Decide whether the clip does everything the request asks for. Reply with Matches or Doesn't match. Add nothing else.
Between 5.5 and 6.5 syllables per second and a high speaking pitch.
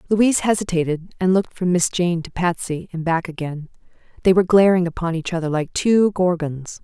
Doesn't match